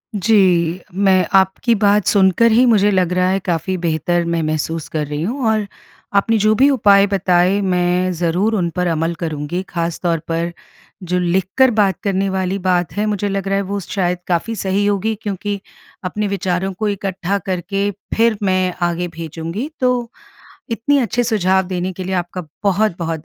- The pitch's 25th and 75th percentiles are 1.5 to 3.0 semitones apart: Yes, average, 2.7 semitones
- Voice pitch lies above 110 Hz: Yes, high, 190 Hz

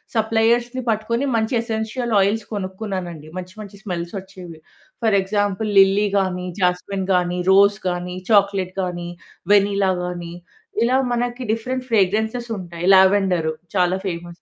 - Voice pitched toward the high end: Yes, high, 195 Hz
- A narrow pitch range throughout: No, average, 3.5 semitones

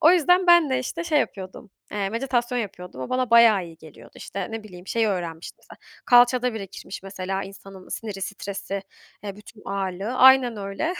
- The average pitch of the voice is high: Yes, high, 210 Hz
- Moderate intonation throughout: Yes, average, 4.5 semitones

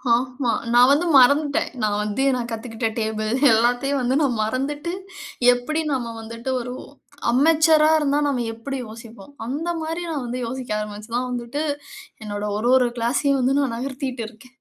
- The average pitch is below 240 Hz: No, very high, 250 Hz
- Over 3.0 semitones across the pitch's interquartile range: Yes, average, 3.5 semitones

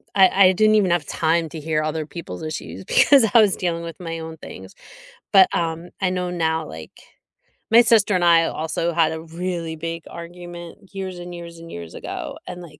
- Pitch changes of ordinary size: No, narrow, 2.2 semitones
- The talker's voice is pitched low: No, medium, 170 Hz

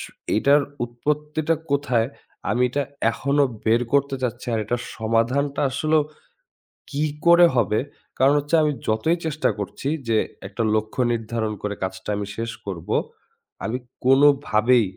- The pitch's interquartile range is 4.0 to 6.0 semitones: Yes, average, 4.6 semitones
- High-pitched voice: No, low, 125 Hz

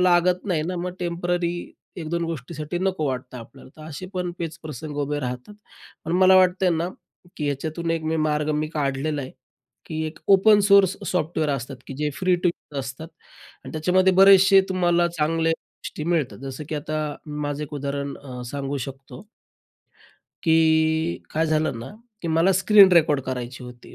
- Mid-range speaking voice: Yes, medium, 160 Hz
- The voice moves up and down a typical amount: Yes, average, 3.4 semitones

